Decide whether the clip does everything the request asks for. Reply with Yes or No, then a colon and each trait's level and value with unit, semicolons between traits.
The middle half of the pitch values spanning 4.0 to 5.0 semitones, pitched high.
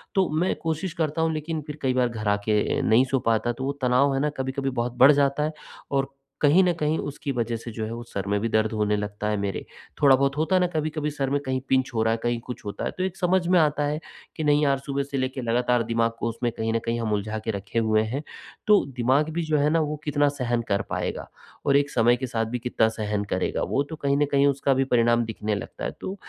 No: average, 4.4 semitones; low, 130 Hz